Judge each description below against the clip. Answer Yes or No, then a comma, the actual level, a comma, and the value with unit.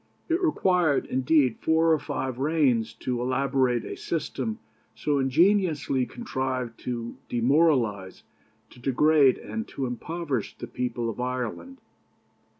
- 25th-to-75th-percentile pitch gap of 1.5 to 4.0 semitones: No, average, 4.5 semitones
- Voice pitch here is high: No, low, 135 Hz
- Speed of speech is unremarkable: No, slow, 120 wpm